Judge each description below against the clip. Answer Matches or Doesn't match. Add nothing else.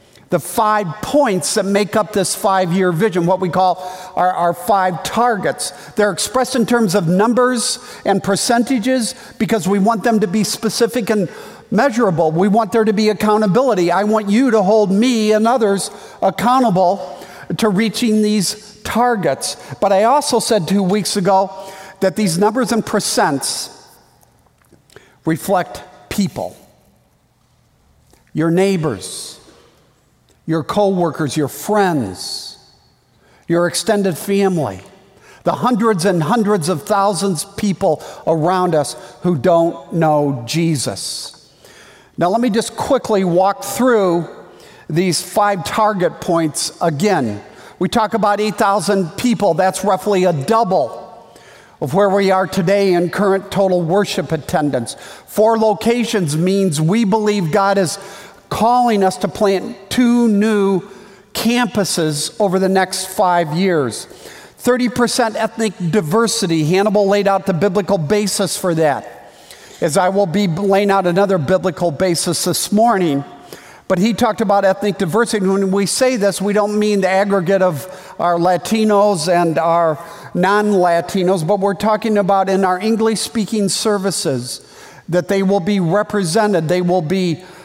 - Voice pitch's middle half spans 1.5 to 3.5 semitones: Matches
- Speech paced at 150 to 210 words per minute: Doesn't match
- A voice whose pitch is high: Matches